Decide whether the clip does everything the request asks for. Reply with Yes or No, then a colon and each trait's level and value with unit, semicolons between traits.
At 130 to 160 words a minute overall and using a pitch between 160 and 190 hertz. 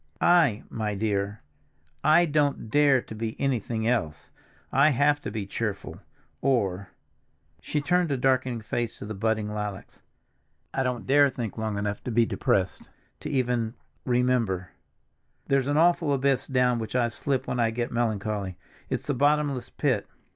No: average, 155 wpm; low, 120 Hz